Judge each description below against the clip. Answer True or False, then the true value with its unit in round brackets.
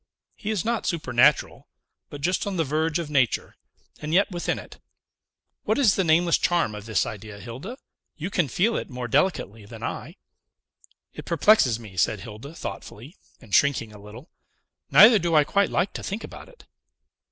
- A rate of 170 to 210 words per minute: True (175 wpm)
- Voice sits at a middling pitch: True (155 Hz)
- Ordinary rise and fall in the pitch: False (8.0 semitones)